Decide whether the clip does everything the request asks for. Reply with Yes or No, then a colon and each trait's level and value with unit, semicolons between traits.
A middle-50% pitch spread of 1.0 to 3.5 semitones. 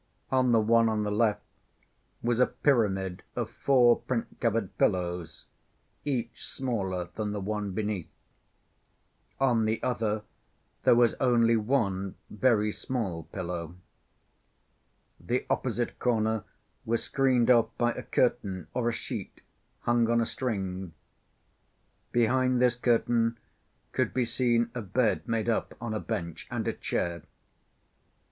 Yes: average, 2.8 semitones